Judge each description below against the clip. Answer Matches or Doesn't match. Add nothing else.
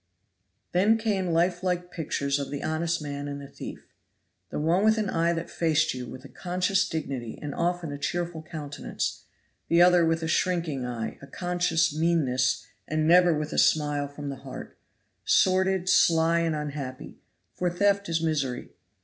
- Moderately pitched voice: Matches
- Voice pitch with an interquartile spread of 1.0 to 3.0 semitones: Doesn't match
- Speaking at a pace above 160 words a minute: Matches